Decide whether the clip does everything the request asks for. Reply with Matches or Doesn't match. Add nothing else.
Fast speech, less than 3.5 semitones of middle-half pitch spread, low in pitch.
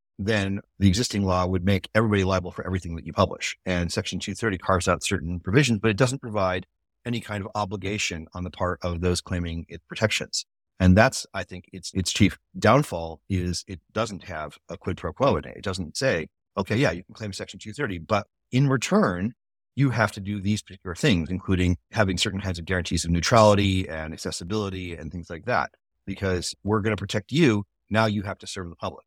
Matches